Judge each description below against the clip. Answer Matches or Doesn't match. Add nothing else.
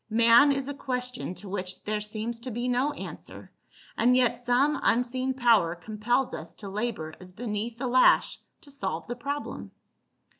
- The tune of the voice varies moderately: Matches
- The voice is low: Doesn't match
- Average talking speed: Matches